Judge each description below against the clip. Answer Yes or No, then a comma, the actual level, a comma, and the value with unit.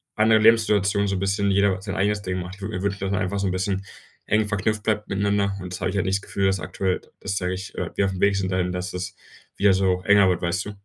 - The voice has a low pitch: Yes, low, 100 Hz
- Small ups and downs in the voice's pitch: Yes, narrow, 1.5 semitones